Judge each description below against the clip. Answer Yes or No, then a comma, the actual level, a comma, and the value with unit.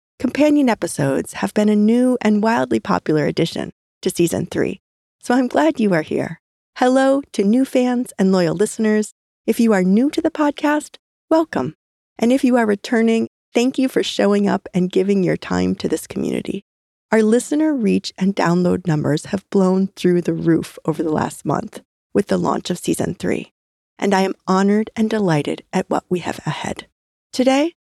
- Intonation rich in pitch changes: Yes, wide, 5.8 semitones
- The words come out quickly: No, average, 180 wpm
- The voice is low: No, high, 210 Hz